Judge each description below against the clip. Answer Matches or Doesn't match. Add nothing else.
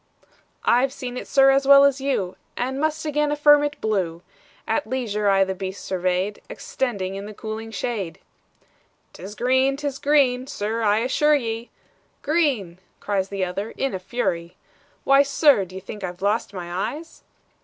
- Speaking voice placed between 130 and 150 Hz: Doesn't match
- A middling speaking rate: Matches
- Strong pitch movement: Matches